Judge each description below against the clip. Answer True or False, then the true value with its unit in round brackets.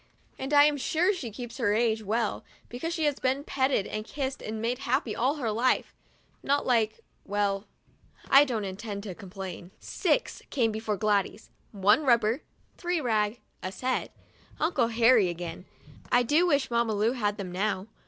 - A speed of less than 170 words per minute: False (175 wpm)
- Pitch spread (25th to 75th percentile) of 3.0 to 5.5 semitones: True (4.3 semitones)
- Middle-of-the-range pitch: False (230 Hz)